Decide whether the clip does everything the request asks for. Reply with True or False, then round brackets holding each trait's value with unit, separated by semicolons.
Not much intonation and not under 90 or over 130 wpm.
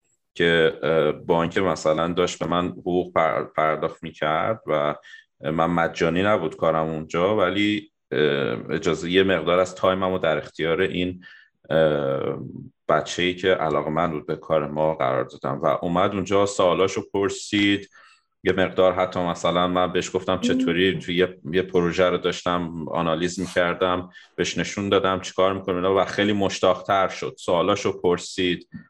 False (1.8 semitones; 140 wpm)